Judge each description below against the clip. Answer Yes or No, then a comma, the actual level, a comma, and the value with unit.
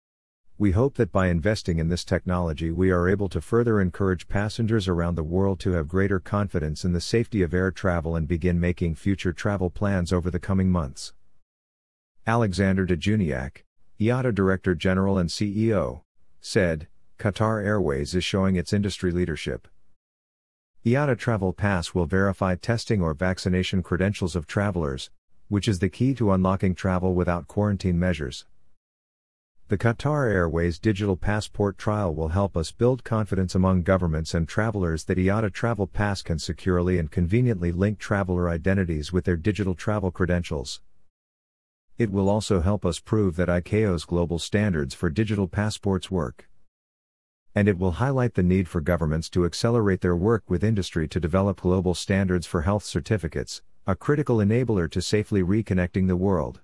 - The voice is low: Yes, very low, 95 Hz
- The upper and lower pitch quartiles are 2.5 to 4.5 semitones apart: Yes, average, 2.8 semitones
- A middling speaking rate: Yes, average, 155 wpm